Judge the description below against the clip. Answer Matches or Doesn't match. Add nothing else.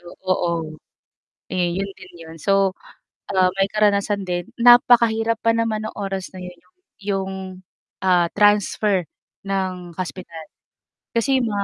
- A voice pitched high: Matches